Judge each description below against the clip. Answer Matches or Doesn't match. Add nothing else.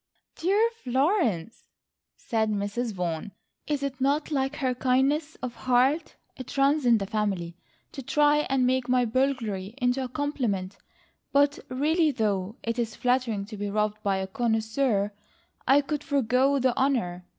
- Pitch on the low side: Doesn't match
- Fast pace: Doesn't match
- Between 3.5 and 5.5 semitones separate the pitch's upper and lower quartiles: Matches